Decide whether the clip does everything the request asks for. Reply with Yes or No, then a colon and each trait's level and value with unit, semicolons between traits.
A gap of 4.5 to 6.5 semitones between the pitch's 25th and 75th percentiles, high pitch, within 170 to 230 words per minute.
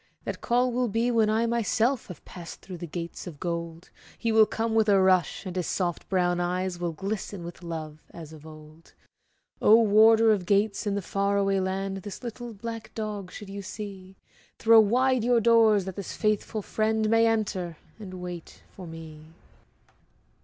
No: average, 3.9 semitones; high, 200 Hz; average, 180 wpm